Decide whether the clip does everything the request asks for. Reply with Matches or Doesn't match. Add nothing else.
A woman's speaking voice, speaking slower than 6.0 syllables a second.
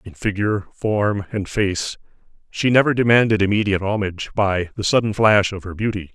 Doesn't match